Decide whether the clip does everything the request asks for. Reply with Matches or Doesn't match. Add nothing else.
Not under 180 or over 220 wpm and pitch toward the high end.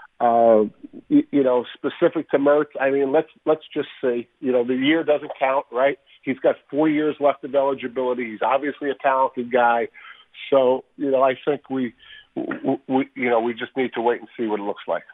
Doesn't match